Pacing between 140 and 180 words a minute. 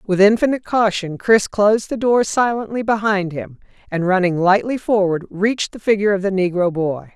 Yes: average, 175 wpm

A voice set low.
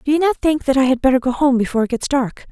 No: very high, 265 Hz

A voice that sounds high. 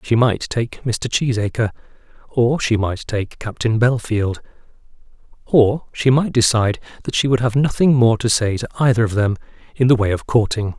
No: low, 115 Hz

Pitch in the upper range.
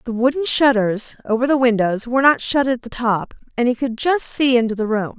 Yes: high, 245 Hz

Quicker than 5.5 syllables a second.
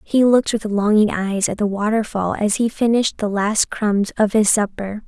No: 4.9 syllables/s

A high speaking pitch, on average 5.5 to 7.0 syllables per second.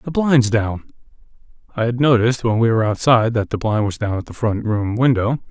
No: low, 115 Hz; 6.0 syllables/s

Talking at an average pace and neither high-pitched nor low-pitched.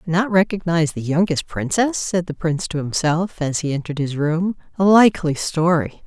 Yes: average, 180 wpm; medium, 170 Hz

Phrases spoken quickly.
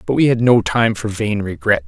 Yes: fast, 255 wpm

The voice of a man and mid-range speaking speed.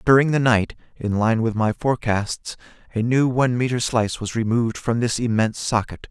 Yes: male; average, 185 wpm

